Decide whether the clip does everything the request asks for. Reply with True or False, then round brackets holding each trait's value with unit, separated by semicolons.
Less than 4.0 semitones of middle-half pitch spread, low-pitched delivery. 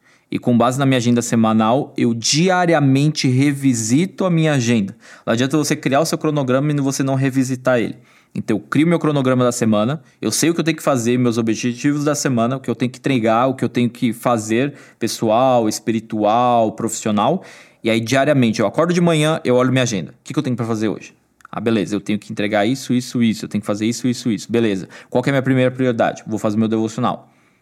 True (3.6 semitones; 125 Hz)